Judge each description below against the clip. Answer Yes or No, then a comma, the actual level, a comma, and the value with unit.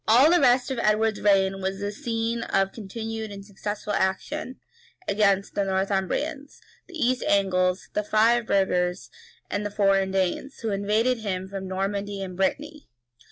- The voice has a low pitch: No, high, 205 Hz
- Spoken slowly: No, average, 155 wpm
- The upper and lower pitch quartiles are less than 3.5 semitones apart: Yes, average, 3.1 semitones